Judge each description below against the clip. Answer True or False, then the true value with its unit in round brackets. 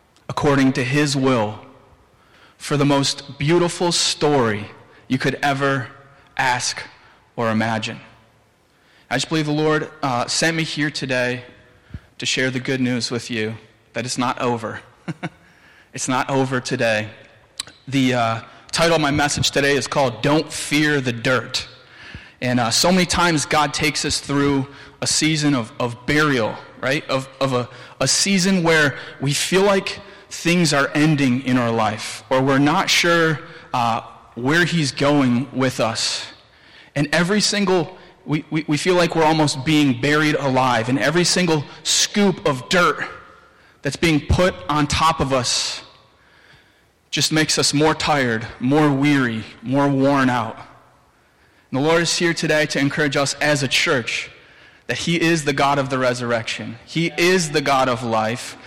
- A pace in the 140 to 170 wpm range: True (160 wpm)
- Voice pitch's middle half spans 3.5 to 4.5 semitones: True (3.9 semitones)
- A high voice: False (140 Hz)